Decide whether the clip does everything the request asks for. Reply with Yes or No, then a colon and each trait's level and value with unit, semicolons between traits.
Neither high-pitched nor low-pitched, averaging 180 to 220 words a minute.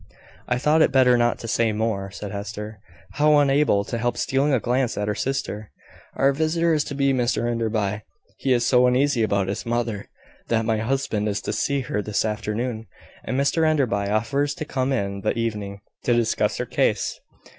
No: low, 120 Hz; average, 190 wpm